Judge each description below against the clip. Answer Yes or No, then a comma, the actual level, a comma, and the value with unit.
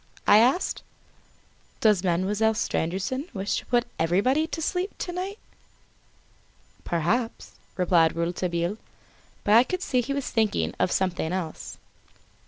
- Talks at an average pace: No, slow, 125 wpm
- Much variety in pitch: Yes, wide, 6.7 semitones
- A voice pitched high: Yes, high, 210 Hz